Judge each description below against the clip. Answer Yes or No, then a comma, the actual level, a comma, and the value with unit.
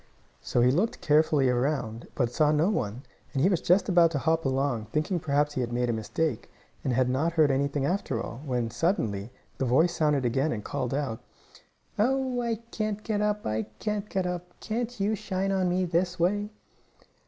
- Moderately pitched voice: Yes, medium, 155 Hz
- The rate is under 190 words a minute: No, average, 200 wpm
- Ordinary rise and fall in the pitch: No, wide, 6.7 semitones